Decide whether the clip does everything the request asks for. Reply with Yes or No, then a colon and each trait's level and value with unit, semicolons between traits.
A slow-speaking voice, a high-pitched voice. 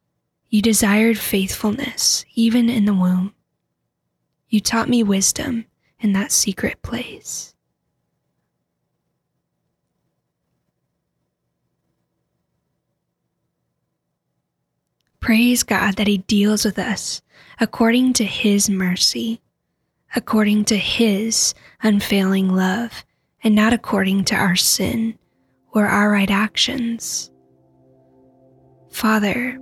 Yes: slow, 85 wpm; high, 205 Hz